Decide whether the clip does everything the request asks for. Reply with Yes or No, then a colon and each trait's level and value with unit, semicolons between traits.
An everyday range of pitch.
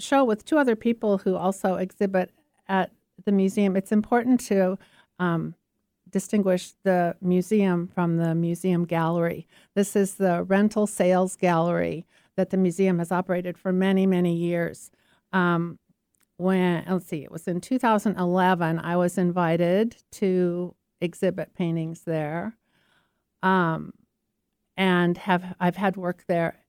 No: narrow, 2.0 semitones